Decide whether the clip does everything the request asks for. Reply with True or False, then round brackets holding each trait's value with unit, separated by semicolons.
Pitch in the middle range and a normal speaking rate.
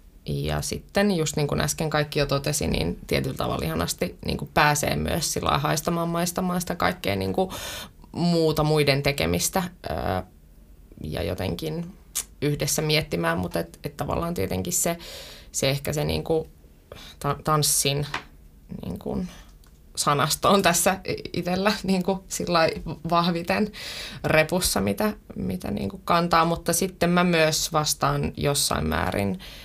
True (150 Hz; 130 wpm)